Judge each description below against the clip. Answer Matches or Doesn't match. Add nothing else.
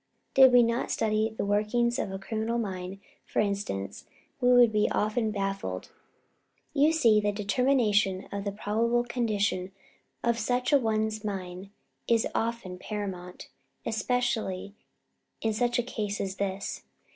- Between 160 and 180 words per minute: Doesn't match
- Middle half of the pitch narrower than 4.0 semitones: Matches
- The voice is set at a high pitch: Matches